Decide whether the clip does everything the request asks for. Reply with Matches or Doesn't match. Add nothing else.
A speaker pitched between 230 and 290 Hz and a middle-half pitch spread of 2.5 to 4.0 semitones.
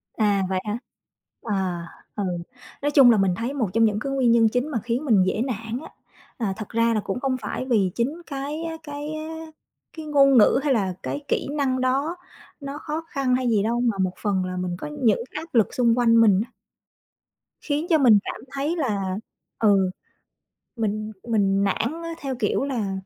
Doesn't match